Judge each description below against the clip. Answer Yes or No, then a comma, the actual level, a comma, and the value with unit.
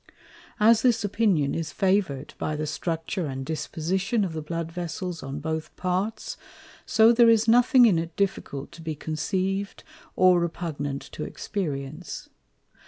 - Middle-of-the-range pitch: Yes, medium, 175 Hz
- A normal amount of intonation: Yes, average, 4.6 semitones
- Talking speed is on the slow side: No, average, 145 wpm